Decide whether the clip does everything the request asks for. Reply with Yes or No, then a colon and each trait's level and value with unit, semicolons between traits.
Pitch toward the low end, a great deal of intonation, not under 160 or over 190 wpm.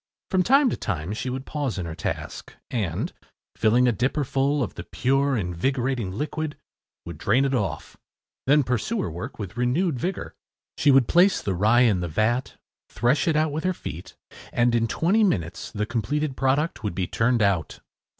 Yes: low, 125 Hz; wide, 6.0 semitones; average, 185 wpm